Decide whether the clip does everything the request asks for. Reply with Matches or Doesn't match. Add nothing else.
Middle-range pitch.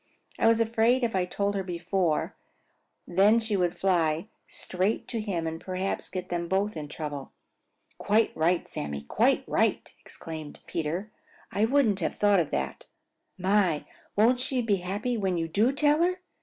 Doesn't match